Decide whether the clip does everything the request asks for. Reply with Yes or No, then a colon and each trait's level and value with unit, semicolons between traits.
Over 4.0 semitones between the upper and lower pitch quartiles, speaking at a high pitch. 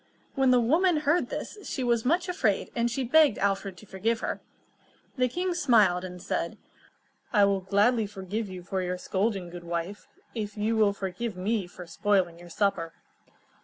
Yes: average, 4.5 semitones; high, 205 Hz